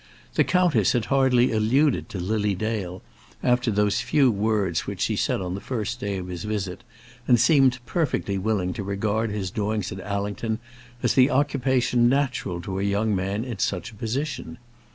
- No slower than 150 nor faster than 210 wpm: Yes, average, 175 wpm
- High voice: No, low, 110 Hz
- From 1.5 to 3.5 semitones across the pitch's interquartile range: No, average, 4.0 semitones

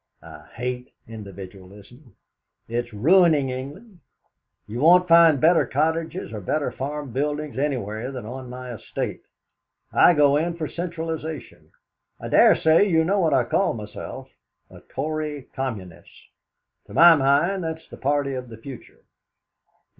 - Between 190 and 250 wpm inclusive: No, average, 140 wpm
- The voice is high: No, medium, 140 Hz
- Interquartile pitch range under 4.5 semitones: No, average, 5.1 semitones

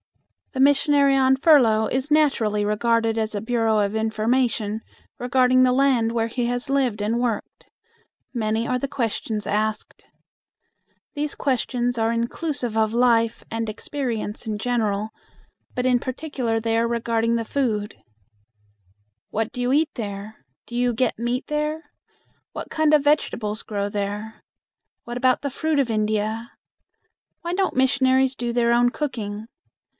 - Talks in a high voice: Yes, high, 235 Hz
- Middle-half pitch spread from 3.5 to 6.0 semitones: No, average, 3.0 semitones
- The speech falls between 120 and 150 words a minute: Yes, average, 145 wpm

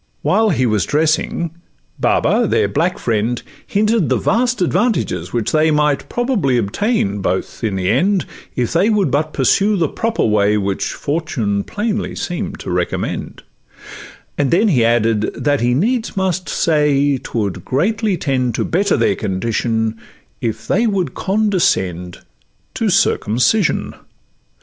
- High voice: No, medium, 145 Hz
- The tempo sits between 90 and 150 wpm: Yes, average, 140 wpm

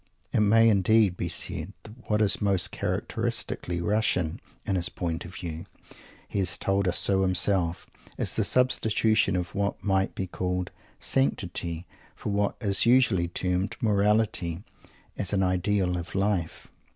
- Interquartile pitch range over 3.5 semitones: No, average, 2.8 semitones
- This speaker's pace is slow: No, average, 150 wpm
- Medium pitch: No, very low, 95 Hz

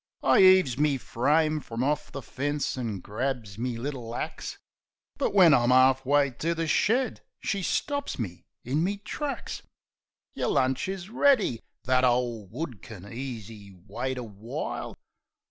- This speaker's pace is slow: No, average, 150 wpm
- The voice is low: Yes, low, 130 Hz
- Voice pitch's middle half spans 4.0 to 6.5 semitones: Yes, average, 5.3 semitones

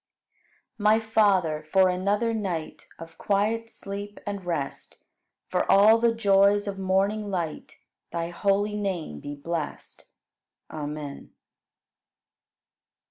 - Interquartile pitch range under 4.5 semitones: Yes, average, 3.8 semitones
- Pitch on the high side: Yes, high, 195 Hz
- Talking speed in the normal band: No, slow, 110 wpm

